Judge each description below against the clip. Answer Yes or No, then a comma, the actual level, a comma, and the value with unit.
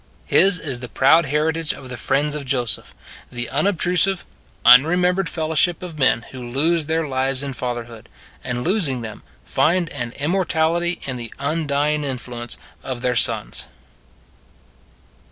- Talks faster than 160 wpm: No, slow, 135 wpm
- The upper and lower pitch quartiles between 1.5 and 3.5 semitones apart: No, average, 4.7 semitones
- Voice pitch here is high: No, medium, 140 Hz